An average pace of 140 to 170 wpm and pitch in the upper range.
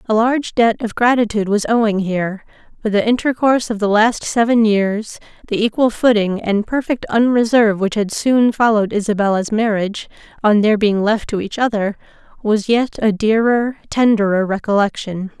Yes: average, 160 wpm; high, 215 Hz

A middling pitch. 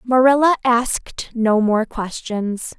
No: high, 235 Hz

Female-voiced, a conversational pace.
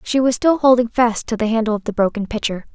No: female; fast, 260 wpm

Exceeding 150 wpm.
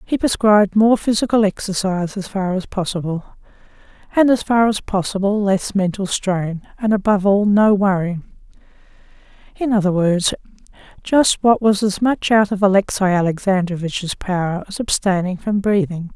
No: average, 140 wpm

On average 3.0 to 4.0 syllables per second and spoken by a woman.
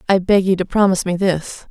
No: 6.0 syllables/s; female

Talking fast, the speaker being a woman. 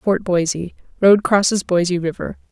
No: slow, 120 wpm; female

